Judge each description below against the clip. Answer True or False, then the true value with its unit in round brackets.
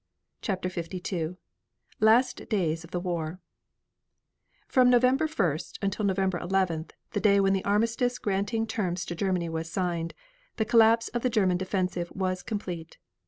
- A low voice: False (190 Hz)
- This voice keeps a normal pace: True (145 wpm)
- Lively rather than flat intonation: False (3.9 semitones)